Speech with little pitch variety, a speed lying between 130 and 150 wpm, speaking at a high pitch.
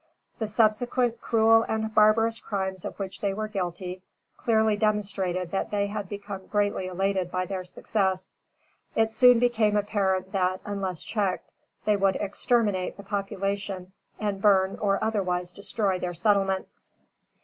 Yes: narrow, 2.2 semitones; average, 140 wpm; high, 200 Hz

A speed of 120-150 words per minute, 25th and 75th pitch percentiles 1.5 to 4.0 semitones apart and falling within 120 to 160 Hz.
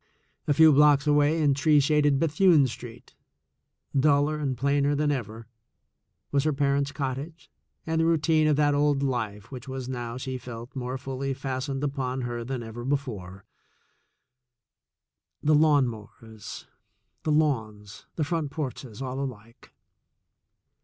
Yes: average, 140 wpm; average, 3.2 semitones; low, 135 Hz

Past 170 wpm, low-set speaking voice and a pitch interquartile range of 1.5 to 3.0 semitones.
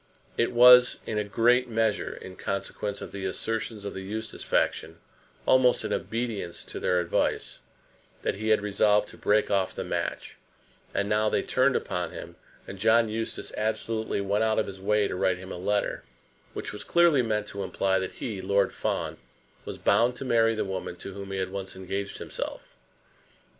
Yes: average, 185 wpm; low, 105 Hz; average, 2.7 semitones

